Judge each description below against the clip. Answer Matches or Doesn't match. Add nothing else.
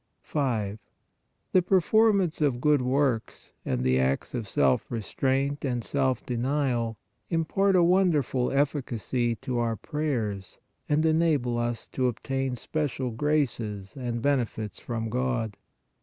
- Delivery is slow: Matches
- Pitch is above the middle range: Doesn't match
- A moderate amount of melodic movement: Matches